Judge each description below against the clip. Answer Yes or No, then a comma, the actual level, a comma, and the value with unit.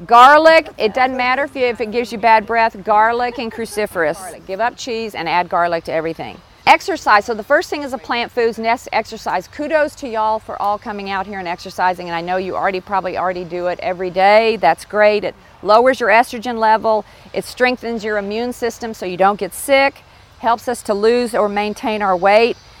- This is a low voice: No, high, 220 Hz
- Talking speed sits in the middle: No, fast, 210 wpm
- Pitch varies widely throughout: No, average, 3.8 semitones